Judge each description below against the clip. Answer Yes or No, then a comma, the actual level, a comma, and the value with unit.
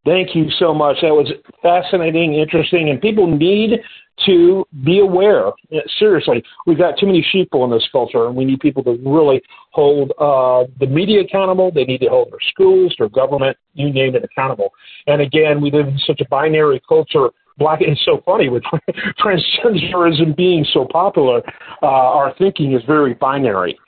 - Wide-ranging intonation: Yes, wide, 5.8 semitones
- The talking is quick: No, average, 175 wpm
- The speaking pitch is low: No, medium, 165 Hz